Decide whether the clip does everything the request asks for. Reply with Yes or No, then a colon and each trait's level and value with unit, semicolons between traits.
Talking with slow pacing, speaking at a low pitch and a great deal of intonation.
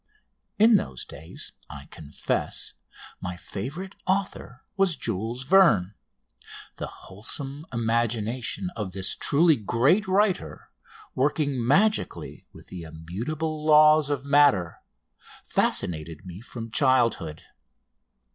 Yes: slow, 100 wpm; low, 125 Hz; wide, 8.1 semitones